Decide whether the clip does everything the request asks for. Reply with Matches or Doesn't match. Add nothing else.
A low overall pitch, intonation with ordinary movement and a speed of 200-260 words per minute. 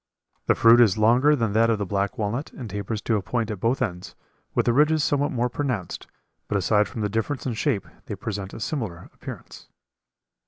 Matches